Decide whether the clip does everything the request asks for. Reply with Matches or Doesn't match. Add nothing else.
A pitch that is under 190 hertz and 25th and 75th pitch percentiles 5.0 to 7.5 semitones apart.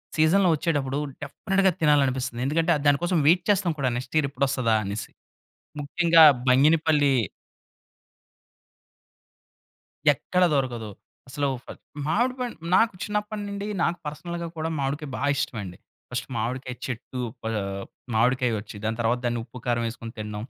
Matches